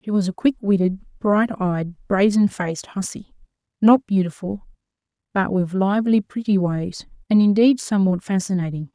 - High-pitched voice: Yes, high, 195 Hz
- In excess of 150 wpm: No, average, 140 wpm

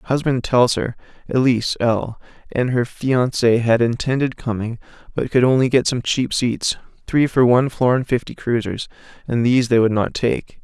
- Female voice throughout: No, male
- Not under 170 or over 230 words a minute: Yes, average, 175 wpm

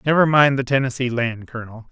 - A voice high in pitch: No, low, 130 Hz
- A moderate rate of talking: Yes, average, 190 wpm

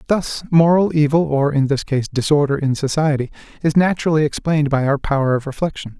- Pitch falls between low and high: Yes, medium, 145 Hz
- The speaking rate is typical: Yes, average, 180 wpm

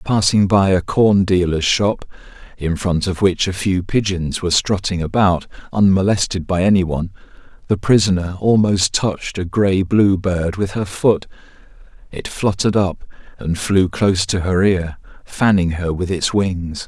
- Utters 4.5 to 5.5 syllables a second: Yes, 4.6 syllables/s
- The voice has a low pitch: Yes, very low, 95 Hz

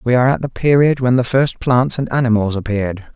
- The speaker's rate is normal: No, fast, 230 wpm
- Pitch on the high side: No, low, 125 Hz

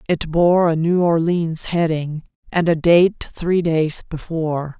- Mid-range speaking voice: Yes, medium, 165 Hz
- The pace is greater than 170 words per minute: No, average, 150 wpm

